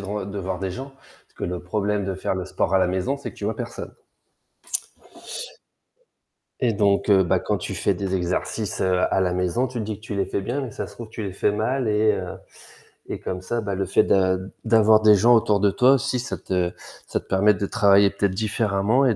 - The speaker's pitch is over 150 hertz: No, low, 100 Hz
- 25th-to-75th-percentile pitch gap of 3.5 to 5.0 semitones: No, average, 2.8 semitones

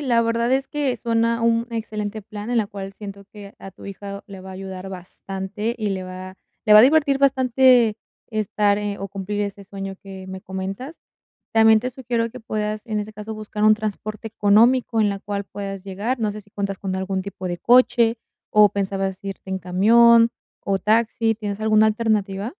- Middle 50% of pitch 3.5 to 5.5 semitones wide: No, average, 2.7 semitones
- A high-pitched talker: Yes, high, 210 Hz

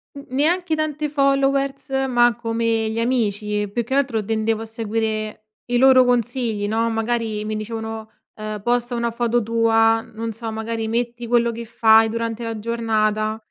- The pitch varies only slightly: Yes, narrow, 1.6 semitones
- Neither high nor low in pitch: No, high, 230 Hz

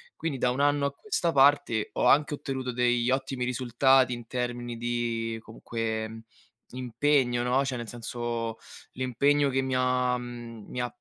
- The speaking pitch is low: Yes, low, 125 Hz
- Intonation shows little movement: Yes, narrow, 2.0 semitones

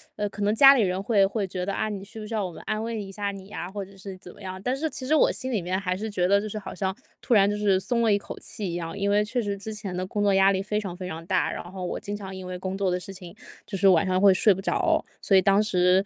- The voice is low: No, high, 200 Hz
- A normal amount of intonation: No, narrow, 2.0 semitones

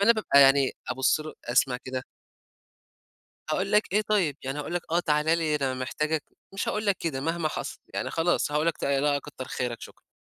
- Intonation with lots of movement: No, average, 4.2 semitones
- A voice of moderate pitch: Yes, medium, 150 Hz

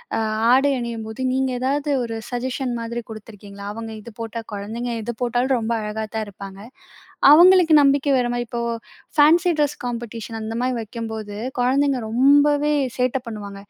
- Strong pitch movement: No, average, 3.5 semitones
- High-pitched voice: Yes, high, 240 Hz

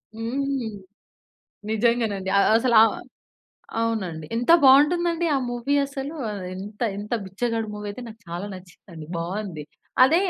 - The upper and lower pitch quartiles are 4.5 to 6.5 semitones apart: Yes, average, 5.2 semitones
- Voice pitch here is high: Yes, high, 225 Hz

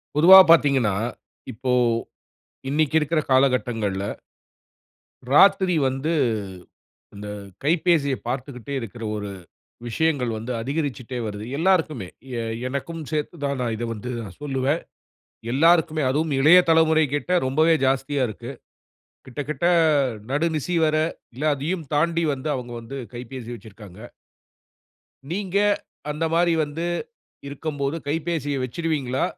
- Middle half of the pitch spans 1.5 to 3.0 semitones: No, average, 4.3 semitones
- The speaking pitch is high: No, medium, 140 Hz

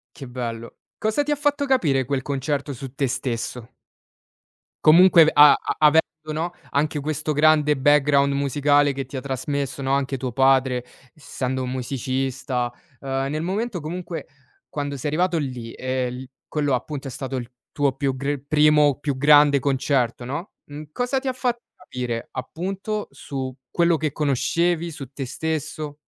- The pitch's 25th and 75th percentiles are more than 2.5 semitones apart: Yes, average, 2.9 semitones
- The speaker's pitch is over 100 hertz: Yes, medium, 140 Hz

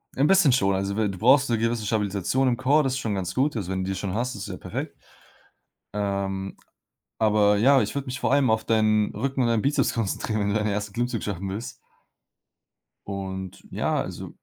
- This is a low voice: Yes, low, 110 Hz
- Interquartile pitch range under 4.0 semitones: No, average, 4.3 semitones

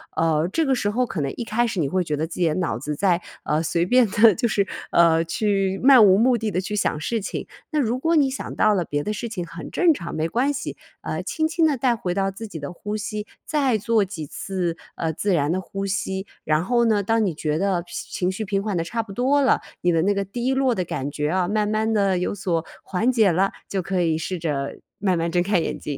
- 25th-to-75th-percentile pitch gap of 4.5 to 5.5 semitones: Yes, average, 5.0 semitones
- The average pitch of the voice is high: Yes, high, 195 Hz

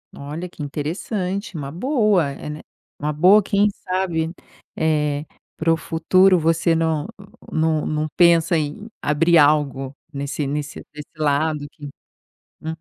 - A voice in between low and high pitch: Yes, medium, 160 Hz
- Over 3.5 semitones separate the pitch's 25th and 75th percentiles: No, average, 2.9 semitones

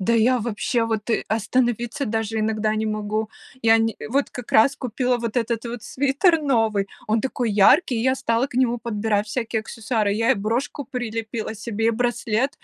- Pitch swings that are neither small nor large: No, narrow, 2.2 semitones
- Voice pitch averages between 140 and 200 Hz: No, high, 230 Hz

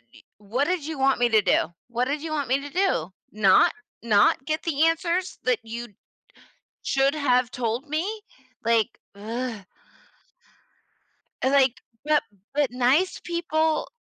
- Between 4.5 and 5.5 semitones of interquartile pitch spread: Yes, average, 4.9 semitones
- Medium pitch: No, very high, 270 Hz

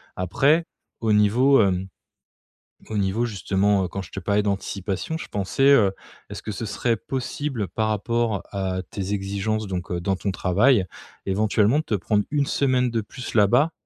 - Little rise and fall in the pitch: No, average, 3.5 semitones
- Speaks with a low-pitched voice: Yes, low, 105 Hz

